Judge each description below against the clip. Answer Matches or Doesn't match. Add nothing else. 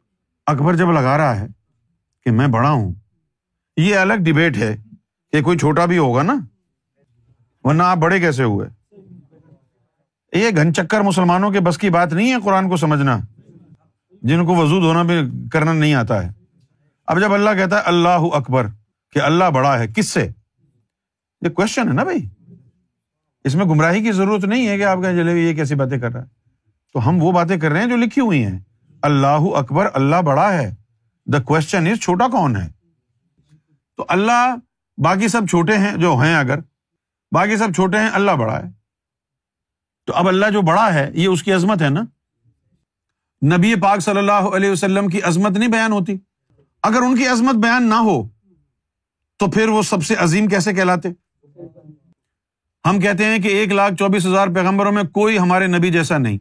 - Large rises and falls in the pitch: Matches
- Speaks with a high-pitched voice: Doesn't match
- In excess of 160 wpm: Matches